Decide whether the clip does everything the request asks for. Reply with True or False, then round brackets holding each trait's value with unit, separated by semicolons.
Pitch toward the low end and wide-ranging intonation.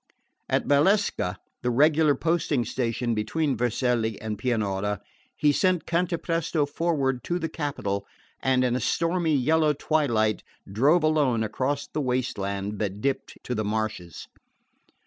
True (130 Hz; 6.1 semitones)